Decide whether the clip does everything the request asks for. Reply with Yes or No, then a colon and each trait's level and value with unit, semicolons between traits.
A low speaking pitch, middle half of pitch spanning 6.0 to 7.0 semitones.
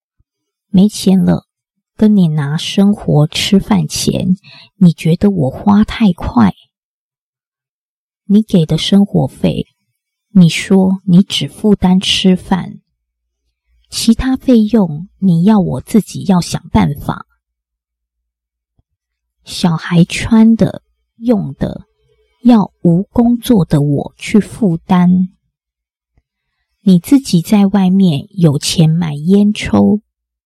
No: medium, 180 Hz; wide, 6.6 semitones